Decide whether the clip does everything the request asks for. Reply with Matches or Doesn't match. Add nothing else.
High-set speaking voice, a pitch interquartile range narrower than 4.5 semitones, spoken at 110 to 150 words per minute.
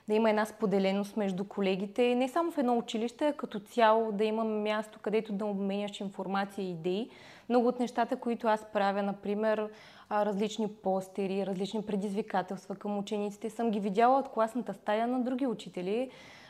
Doesn't match